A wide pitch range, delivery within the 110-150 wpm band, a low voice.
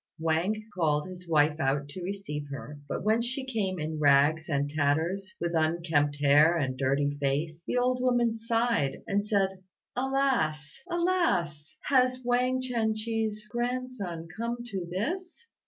No: wide, 8.1 semitones; average, 145 wpm; medium, 185 Hz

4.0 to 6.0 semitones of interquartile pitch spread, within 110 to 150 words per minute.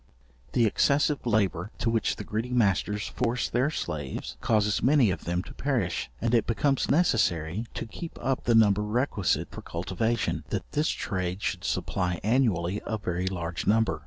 No: average, 4.8 semitones; average, 165 wpm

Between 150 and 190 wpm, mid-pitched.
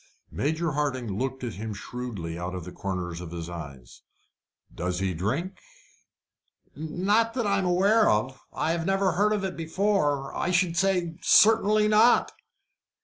Yes: average, 155 wpm; medium, 155 Hz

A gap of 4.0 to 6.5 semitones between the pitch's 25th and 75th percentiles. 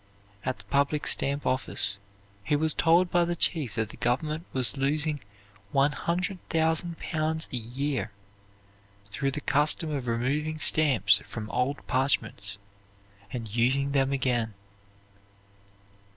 Yes: average, 4.3 semitones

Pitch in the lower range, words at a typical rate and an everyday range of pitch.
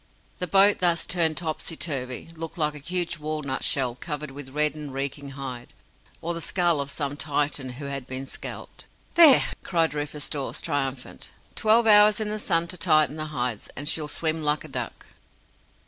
No: medium, 150 Hz; average, 180 wpm; average, 3.3 semitones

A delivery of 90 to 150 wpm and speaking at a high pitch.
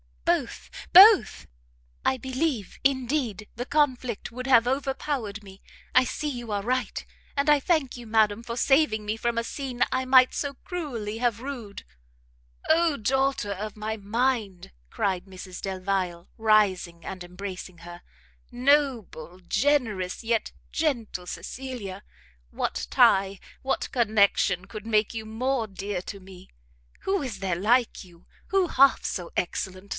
Yes: average, 140 wpm; high, 225 Hz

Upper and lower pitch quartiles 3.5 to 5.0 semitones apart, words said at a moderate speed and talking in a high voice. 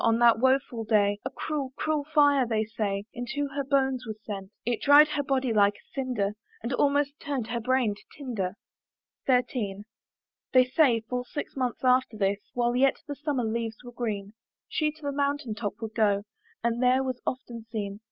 Yes: average, 3.8 semitones; average, 185 wpm; high, 245 Hz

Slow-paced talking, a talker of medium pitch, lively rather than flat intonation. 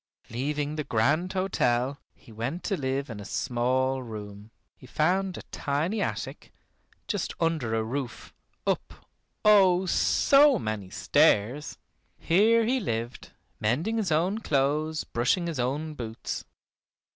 Yes: slow, 130 wpm; medium, 145 Hz; wide, 7.1 semitones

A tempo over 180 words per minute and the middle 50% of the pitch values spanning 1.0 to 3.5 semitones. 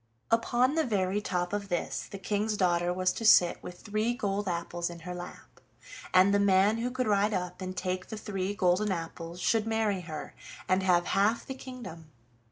Yes: average, 190 wpm; average, 3.1 semitones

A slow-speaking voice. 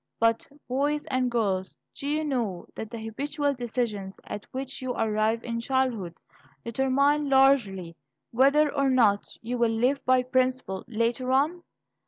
No: average, 145 wpm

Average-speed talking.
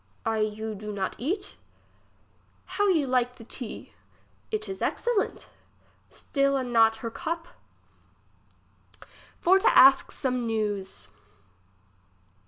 No: slow, 110 wpm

